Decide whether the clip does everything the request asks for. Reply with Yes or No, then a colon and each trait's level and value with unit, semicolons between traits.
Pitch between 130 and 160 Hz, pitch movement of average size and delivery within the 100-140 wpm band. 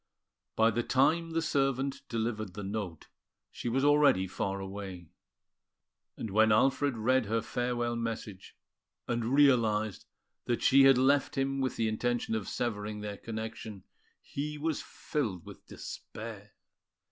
No: low, 115 Hz; average, 4.3 semitones; slow, 135 wpm